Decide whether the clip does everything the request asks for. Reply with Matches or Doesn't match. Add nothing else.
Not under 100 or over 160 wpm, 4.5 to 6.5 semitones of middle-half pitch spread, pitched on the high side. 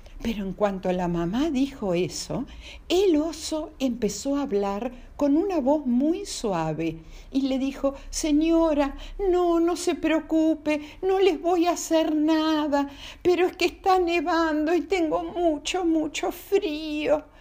Doesn't match